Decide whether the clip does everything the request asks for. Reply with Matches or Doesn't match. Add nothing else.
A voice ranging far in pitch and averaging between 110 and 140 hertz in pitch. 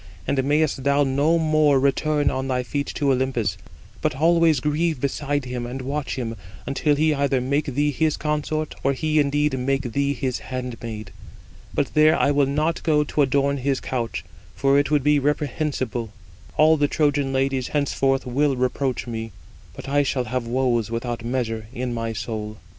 Doesn't match